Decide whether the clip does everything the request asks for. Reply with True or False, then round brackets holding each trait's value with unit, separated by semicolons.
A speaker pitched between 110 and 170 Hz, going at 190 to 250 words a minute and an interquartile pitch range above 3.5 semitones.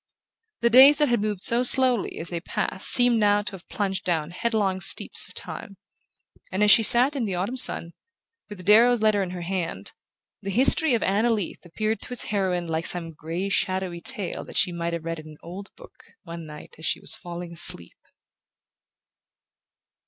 False (195 Hz; 195 wpm; 4.9 semitones)